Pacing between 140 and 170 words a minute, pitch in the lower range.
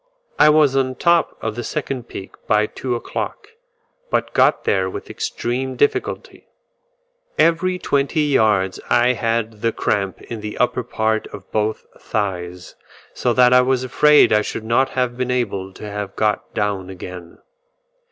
Yes: average, 160 wpm; low, 115 Hz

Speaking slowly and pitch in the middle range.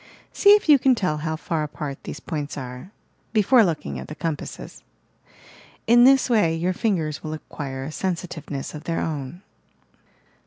No: average, 165 wpm; medium, 165 Hz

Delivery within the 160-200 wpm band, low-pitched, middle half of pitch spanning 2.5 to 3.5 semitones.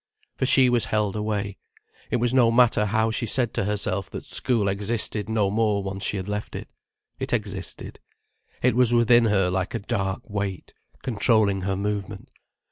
Yes: average, 175 wpm; low, 105 Hz; average, 2.9 semitones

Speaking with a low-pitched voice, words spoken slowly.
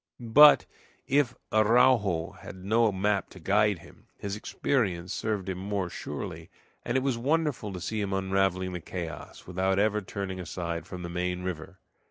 No: very low, 95 Hz; average, 165 wpm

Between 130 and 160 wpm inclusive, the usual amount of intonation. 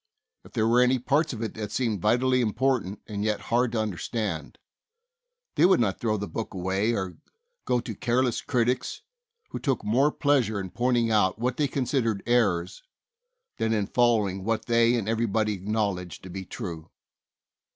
No: average, 170 wpm; average, 3.3 semitones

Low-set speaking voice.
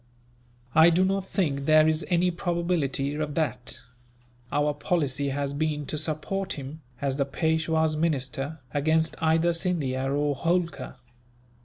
No: medium, 155 Hz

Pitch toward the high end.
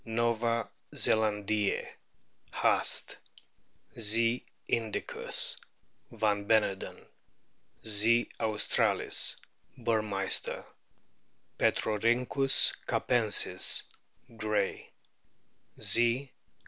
No: low, 110 Hz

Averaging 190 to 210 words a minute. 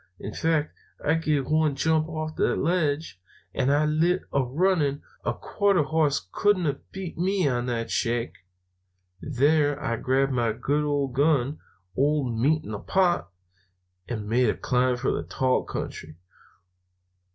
No: average, 150 wpm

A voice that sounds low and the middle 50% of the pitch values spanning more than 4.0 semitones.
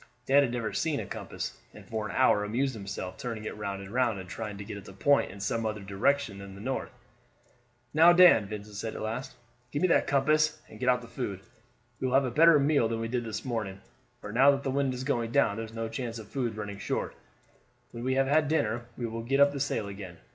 Yes: low, 115 Hz; average, 4.5 semitones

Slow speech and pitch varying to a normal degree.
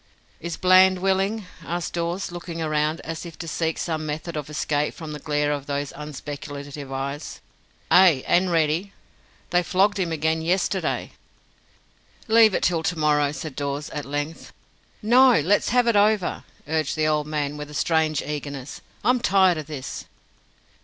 No: average, 160 wpm; average, 3.6 semitones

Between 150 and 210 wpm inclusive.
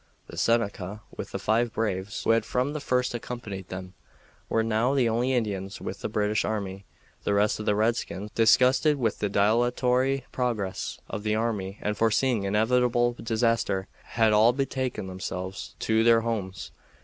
Yes: average, 160 wpm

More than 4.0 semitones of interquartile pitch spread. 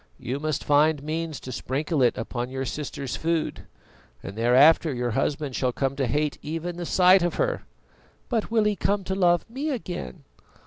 Yes: average, 5.0 semitones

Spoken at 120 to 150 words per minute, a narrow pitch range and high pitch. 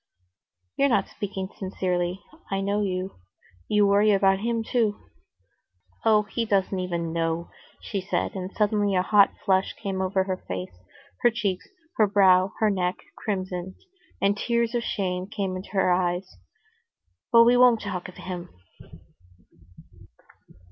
Yes: average, 140 wpm; narrow, 2.3 semitones; high, 195 Hz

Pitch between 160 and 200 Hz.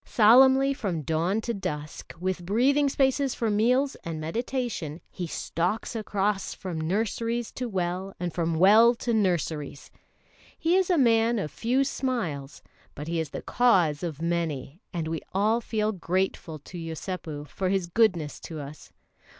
Yes: high, 190 Hz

